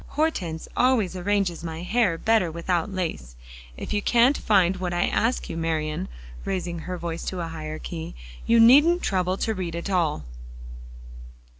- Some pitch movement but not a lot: Yes, average, 4.2 semitones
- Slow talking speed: No, average, 160 wpm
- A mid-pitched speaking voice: Yes, medium, 180 Hz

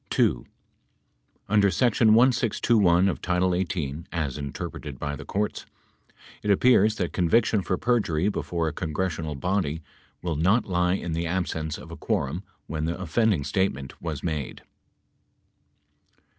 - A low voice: Yes, very low, 90 Hz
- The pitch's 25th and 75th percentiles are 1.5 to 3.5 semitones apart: No, average, 4.3 semitones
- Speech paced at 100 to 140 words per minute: Yes, slow, 135 wpm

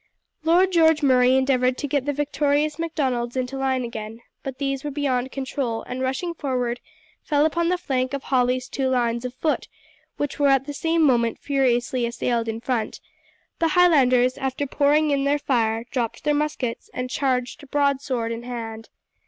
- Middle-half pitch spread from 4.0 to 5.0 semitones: No, average, 2.8 semitones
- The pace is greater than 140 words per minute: Yes, average, 170 wpm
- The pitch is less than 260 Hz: No, very high, 265 Hz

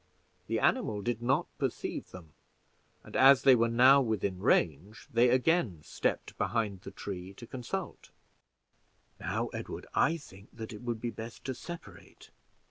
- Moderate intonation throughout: Yes, average, 4.2 semitones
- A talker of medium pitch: No, low, 115 Hz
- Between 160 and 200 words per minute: No, average, 150 wpm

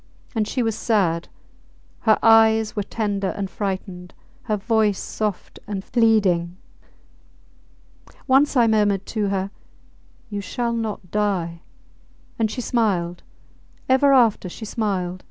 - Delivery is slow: Yes, slow, 120 wpm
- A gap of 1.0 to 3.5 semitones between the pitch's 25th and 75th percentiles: Yes, average, 2.8 semitones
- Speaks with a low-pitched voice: No, high, 210 Hz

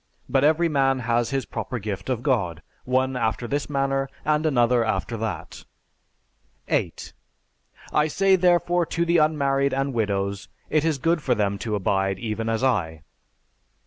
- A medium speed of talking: Yes, average, 155 wpm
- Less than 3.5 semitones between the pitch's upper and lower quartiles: No, average, 5.2 semitones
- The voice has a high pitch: No, low, 130 Hz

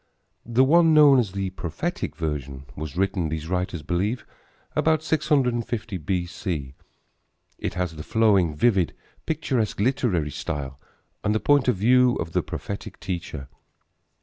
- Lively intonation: Yes, wide, 7.4 semitones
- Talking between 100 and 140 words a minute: Yes, slow, 135 wpm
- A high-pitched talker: No, very low, 95 Hz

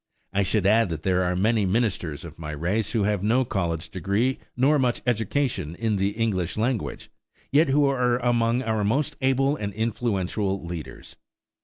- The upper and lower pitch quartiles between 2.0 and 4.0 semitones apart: No, average, 4.6 semitones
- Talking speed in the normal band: Yes, average, 170 wpm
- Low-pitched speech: Yes, low, 110 Hz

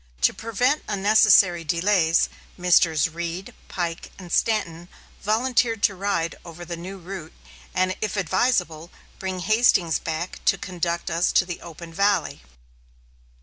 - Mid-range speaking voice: Yes, medium, 180 Hz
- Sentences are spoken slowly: Yes, slow, 130 wpm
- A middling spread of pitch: Yes, average, 3.3 semitones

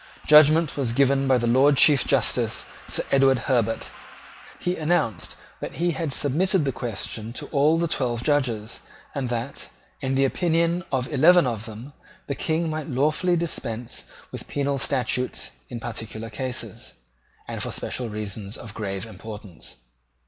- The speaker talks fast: No, average, 150 wpm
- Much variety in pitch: No, average, 4.8 semitones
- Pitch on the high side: No, low, 130 Hz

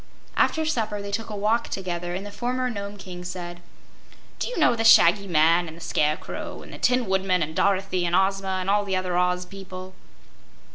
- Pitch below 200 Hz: Yes, high, 190 Hz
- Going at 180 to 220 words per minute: Yes, average, 200 wpm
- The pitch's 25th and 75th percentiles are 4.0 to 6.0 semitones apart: No, narrow, 2.5 semitones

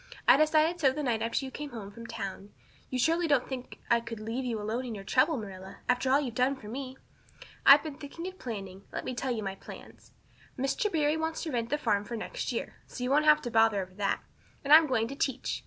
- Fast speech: Yes, fast, 245 wpm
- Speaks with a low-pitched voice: No, very high, 255 Hz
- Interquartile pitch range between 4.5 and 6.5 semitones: Yes, average, 4.8 semitones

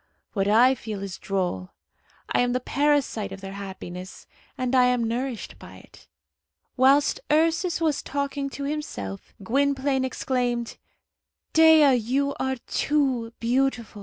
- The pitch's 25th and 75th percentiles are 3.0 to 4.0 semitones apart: No, average, 4.7 semitones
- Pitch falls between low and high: No, very high, 255 Hz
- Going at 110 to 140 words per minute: Yes, slow, 135 wpm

